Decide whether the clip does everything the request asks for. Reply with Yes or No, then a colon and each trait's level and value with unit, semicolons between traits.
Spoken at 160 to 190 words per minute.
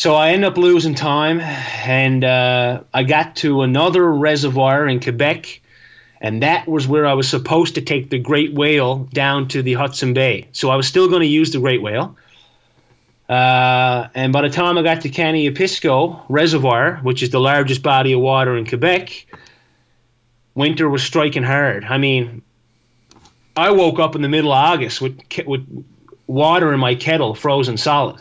Yes: average, 180 wpm